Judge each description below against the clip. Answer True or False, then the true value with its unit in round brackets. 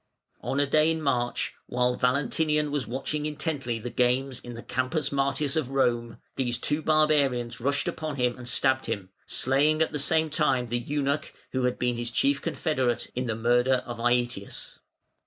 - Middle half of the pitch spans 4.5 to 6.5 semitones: False (3.4 semitones)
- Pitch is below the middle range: True (130 Hz)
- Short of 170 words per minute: False (175 wpm)